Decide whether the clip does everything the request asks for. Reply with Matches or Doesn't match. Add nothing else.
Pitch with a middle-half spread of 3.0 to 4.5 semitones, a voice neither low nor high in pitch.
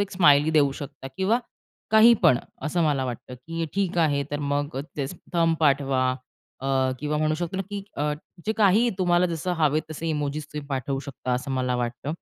Matches